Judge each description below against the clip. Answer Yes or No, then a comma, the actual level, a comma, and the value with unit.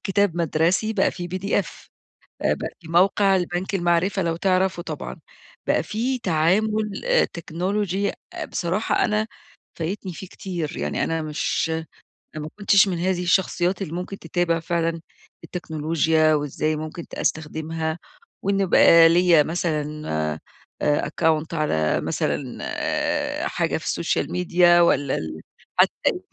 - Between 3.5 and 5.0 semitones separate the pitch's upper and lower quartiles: No, average, 3.0 semitones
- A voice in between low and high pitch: Yes, medium, 175 Hz